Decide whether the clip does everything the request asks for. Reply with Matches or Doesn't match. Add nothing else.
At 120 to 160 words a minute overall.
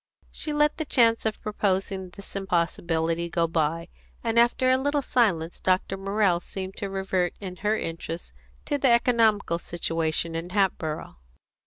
Matches